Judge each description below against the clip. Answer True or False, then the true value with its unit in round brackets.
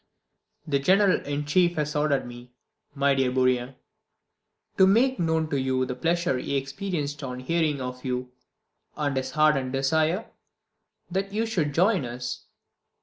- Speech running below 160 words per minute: True (145 wpm)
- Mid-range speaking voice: True (145 Hz)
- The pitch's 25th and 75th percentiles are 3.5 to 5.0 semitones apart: True (4.6 semitones)